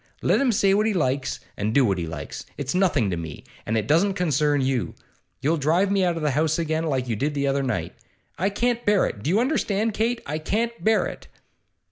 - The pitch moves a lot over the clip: Yes, wide, 7.1 semitones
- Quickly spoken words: Yes, fast, 230 wpm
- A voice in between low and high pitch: Yes, medium, 155 Hz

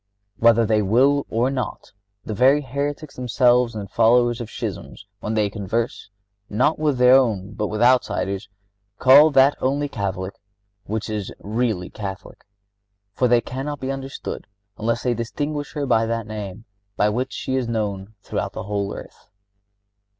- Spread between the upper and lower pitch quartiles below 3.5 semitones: No, average, 3.8 semitones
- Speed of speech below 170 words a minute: Yes, average, 155 wpm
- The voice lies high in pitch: No, low, 115 Hz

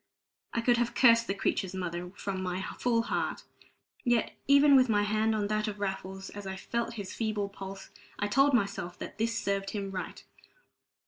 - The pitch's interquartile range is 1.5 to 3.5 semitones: Yes, average, 3.1 semitones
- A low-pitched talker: No, high, 205 Hz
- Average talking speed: Yes, average, 185 wpm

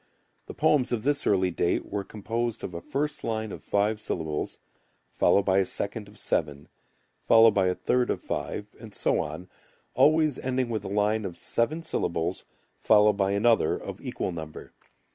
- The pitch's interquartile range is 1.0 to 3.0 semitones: No, average, 4.0 semitones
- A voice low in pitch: Yes, low, 105 Hz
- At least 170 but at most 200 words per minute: Yes, average, 175 wpm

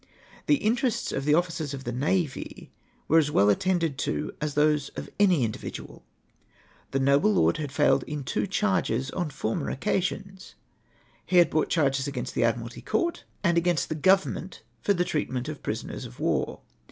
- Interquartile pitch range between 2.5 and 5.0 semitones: No, wide, 5.4 semitones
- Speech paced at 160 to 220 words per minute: Yes, average, 175 wpm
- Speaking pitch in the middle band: Yes, medium, 155 Hz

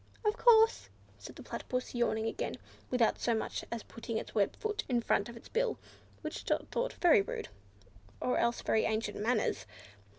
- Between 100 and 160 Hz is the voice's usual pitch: No, high, 235 Hz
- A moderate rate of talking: Yes, average, 175 wpm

